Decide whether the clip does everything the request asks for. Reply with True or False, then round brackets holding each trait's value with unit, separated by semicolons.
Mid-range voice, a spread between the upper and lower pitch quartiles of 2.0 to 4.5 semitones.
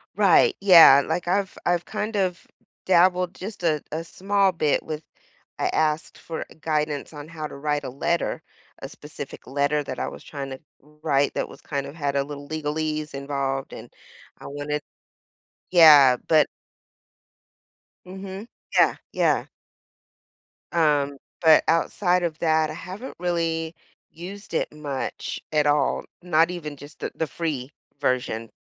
True (155 Hz; 3.2 semitones)